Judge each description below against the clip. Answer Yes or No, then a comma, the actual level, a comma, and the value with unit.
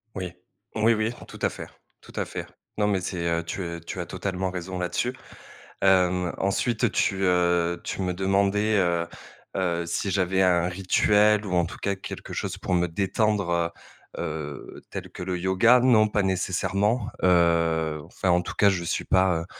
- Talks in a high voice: No, very low, 95 Hz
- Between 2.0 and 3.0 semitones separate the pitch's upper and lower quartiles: Yes, narrow, 2.4 semitones